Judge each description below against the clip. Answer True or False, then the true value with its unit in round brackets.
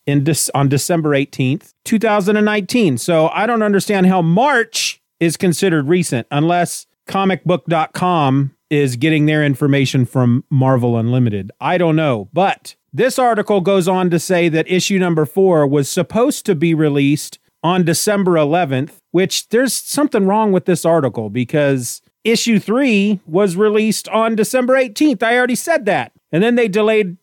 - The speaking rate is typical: True (150 wpm)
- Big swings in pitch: True (6.2 semitones)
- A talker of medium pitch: True (180 Hz)